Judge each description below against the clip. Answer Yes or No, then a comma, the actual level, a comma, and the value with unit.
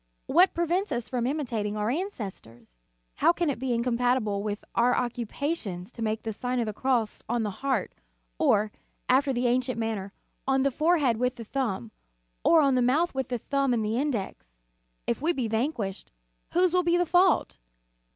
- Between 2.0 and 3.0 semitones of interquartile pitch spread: No, average, 4.4 semitones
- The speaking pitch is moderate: No, high, 245 Hz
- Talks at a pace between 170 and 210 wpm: Yes, average, 180 wpm